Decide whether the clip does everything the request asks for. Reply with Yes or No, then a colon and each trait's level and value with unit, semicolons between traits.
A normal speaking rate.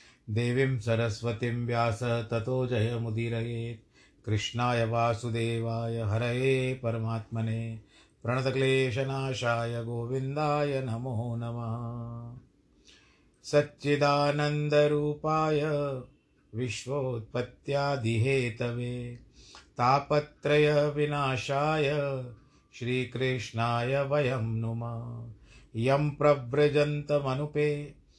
No: slow, 45 wpm